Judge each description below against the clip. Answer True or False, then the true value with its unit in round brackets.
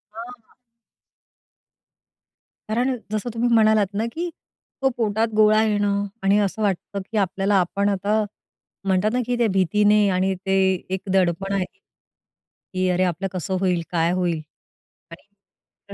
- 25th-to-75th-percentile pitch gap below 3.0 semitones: True (2.5 semitones)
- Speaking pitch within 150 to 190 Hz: False (200 Hz)